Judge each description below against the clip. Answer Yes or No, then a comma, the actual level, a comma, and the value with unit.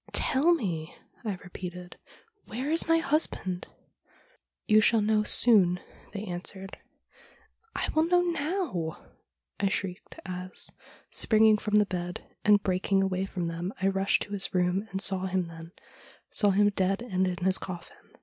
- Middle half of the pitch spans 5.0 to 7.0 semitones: No, average, 3.2 semitones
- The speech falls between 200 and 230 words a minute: No, average, 170 wpm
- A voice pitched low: No, high, 195 Hz